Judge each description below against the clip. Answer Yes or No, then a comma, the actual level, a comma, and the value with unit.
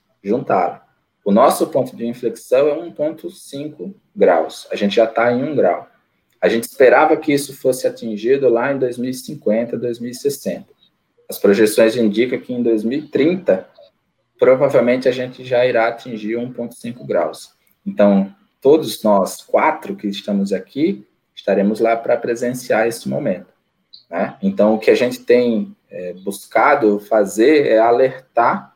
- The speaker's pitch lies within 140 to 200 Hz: No, low, 120 Hz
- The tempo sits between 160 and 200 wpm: No, average, 140 wpm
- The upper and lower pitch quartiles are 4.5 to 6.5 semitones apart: No, average, 3.6 semitones